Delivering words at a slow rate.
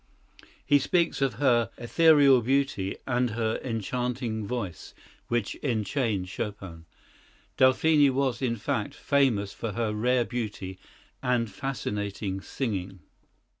Yes: slow, 110 wpm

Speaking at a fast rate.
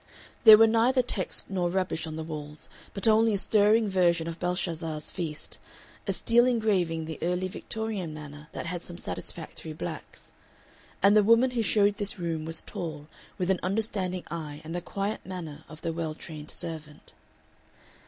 No: average, 175 wpm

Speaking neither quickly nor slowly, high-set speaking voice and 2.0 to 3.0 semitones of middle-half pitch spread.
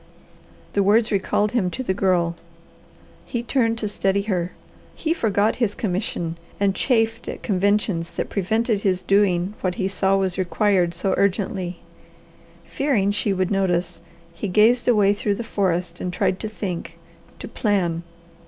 Yes: average, 155 wpm; high, 195 Hz; average, 2.7 semitones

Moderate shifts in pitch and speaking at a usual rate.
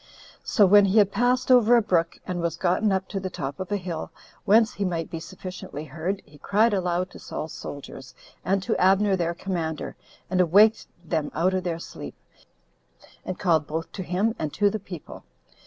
Yes: average, 3.5 semitones; average, 195 wpm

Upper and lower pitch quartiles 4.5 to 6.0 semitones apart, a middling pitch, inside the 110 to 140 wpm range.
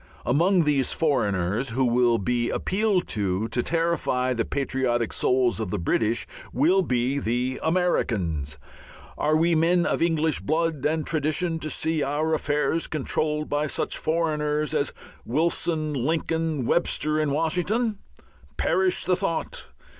Yes: average, 4.8 semitones; medium, 150 Hz; slow, 135 wpm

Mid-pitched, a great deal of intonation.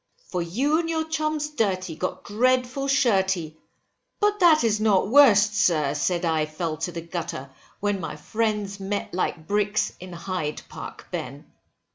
No: high, 200 Hz; wide, 6.7 semitones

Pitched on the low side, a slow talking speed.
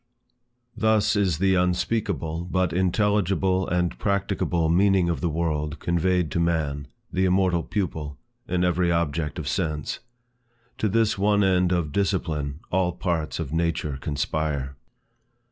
Yes: very low, 85 Hz; slow, 130 wpm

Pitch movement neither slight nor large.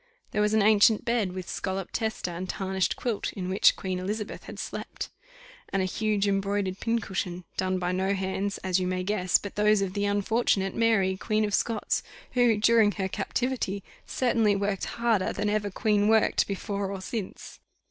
No: narrow, 2.2 semitones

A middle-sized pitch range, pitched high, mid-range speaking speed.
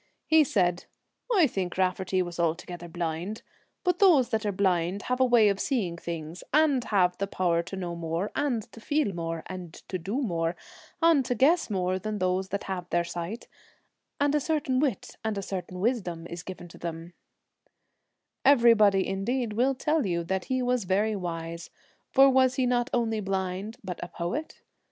No: wide, 6.1 semitones; high, 195 Hz; average, 185 wpm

